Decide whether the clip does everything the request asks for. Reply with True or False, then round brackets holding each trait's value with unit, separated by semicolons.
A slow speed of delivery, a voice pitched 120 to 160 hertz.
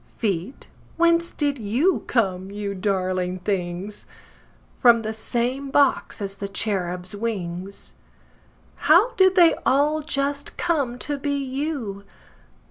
False (110 wpm; 230 Hz)